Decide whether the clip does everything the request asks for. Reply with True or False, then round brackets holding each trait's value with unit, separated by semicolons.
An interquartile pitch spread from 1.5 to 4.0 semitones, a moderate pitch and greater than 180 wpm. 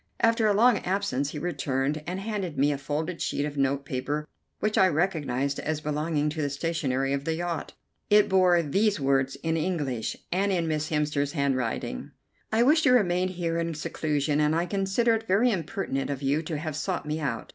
False (4.7 semitones; 155 Hz; 200 wpm)